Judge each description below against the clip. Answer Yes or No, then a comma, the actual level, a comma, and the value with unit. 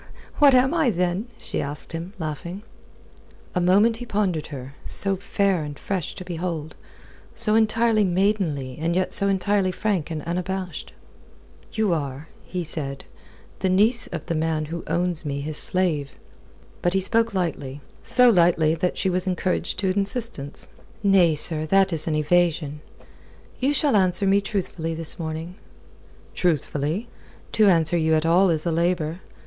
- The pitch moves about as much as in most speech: Yes, average, 3.8 semitones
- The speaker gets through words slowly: No, average, 155 wpm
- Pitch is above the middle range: No, medium, 175 Hz